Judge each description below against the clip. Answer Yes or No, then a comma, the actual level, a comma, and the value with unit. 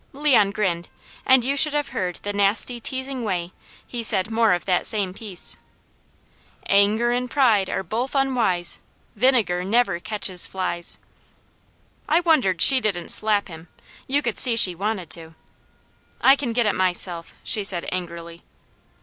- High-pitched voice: Yes, high, 210 Hz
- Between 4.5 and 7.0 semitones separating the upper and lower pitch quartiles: Yes, average, 5.3 semitones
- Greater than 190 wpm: No, average, 155 wpm